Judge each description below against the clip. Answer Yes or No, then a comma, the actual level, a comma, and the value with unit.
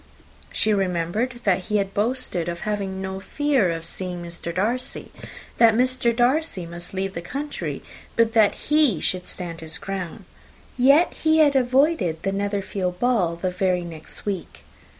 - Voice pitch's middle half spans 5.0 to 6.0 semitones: Yes, wide, 5.6 semitones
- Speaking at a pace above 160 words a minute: No, average, 155 wpm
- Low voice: No, high, 195 Hz